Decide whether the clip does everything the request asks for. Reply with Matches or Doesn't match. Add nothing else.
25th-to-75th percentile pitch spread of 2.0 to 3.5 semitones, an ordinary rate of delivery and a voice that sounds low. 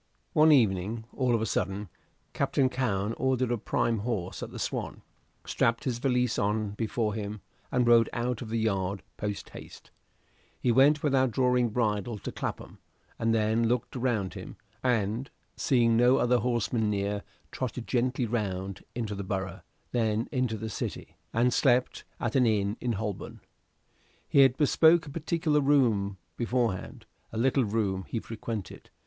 Matches